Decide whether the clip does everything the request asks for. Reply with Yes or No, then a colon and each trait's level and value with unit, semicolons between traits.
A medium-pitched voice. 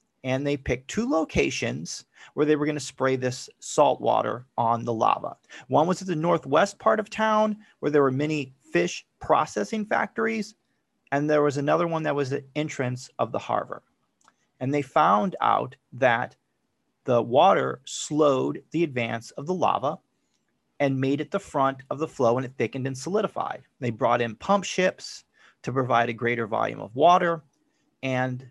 Yes: medium, 145 Hz